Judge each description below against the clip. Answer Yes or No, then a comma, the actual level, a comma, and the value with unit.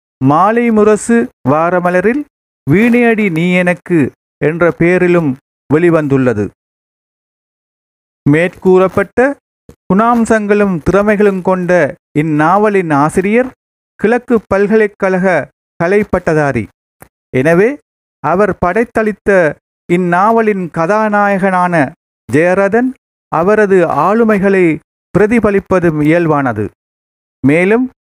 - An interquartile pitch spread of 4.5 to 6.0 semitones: Yes, average, 4.9 semitones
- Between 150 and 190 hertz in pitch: Yes, medium, 185 Hz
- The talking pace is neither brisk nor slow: No, slow, 60 wpm